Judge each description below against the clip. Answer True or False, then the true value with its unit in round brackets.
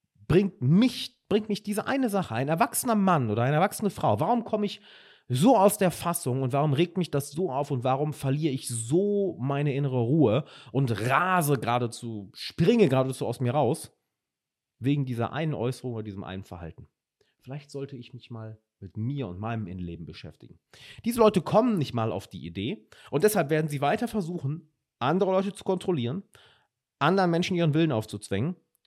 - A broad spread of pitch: True (7.3 semitones)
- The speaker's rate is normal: True (180 wpm)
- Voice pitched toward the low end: False (145 Hz)